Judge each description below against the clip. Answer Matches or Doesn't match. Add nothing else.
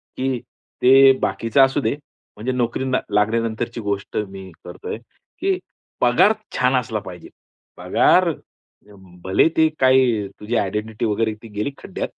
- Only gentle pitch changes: Doesn't match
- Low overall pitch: Matches